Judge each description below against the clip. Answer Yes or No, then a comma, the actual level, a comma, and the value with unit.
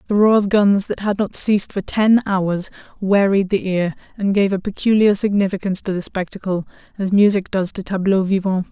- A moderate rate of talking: Yes, average, 195 wpm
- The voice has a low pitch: No, high, 195 Hz